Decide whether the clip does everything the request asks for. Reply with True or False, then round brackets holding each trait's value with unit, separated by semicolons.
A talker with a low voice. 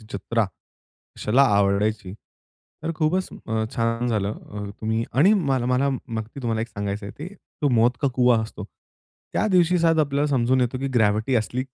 True (120 Hz)